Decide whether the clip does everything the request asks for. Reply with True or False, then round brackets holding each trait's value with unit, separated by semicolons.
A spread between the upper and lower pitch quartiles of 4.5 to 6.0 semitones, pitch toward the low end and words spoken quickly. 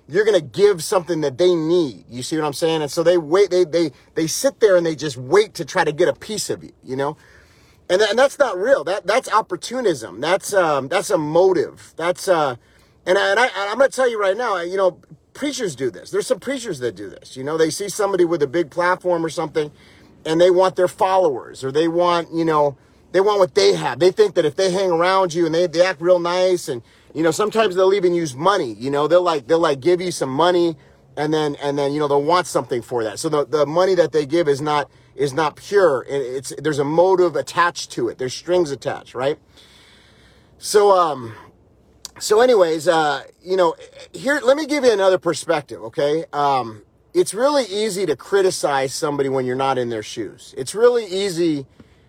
False (5.0 semitones; 175 Hz; 225 wpm)